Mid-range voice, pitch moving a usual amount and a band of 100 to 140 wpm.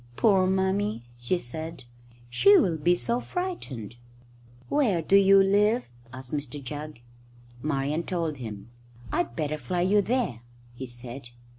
No: medium, 160 Hz; wide, 7.3 semitones; slow, 135 wpm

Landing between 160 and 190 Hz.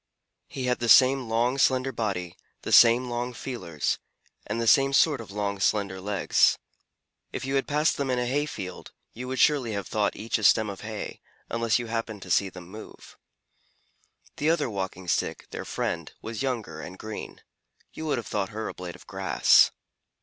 No: low, 115 Hz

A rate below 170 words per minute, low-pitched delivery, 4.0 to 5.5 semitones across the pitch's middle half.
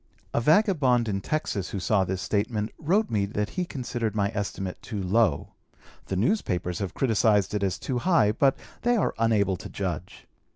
No: average, 175 wpm; low, 105 Hz; average, 5.0 semitones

